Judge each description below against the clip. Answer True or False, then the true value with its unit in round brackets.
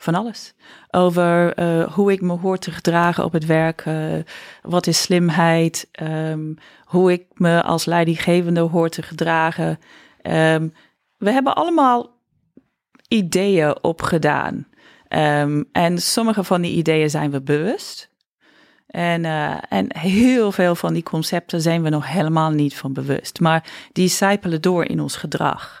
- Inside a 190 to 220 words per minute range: False (145 wpm)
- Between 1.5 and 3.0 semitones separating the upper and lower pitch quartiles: True (2.4 semitones)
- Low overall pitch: False (170 Hz)